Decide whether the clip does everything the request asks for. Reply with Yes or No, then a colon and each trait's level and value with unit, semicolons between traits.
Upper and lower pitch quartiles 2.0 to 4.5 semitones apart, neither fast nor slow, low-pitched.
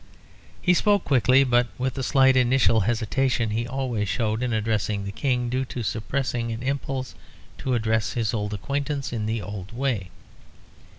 Yes: average, 3.2 semitones; average, 165 wpm; low, 120 Hz